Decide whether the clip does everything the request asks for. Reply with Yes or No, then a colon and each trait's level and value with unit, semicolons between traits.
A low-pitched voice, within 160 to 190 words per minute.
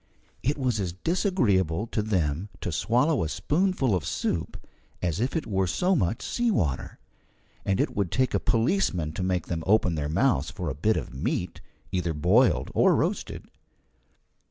Yes: low, 100 Hz; average, 170 wpm